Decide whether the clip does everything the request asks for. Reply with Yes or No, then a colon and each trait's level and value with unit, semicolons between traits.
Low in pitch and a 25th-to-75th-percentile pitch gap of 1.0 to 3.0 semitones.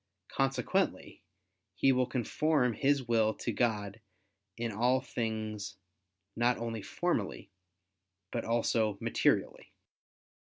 Yes: low, 115 Hz; narrow, 2.6 semitones